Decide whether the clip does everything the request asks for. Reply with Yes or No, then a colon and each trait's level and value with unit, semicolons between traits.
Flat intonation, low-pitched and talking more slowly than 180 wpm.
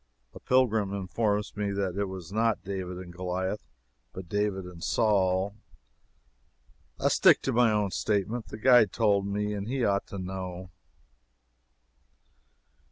Yes: narrow, 2.2 semitones; low, 100 Hz; average, 140 wpm